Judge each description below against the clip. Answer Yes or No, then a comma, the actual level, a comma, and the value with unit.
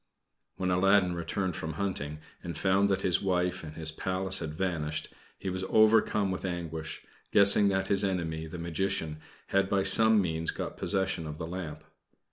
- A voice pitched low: Yes, very low, 90 Hz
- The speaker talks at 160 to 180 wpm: Yes, average, 170 wpm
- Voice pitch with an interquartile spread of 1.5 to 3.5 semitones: Yes, average, 3.1 semitones